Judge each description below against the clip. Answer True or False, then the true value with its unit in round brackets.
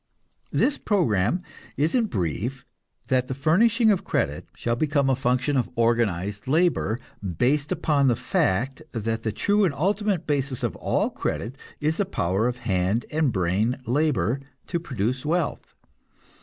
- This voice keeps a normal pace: True (150 wpm)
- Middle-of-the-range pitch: False (130 Hz)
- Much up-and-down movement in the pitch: True (5.7 semitones)